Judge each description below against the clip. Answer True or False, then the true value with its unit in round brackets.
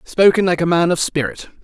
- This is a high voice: False (175 Hz)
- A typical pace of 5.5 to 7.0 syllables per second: True (5.7 syllables/s)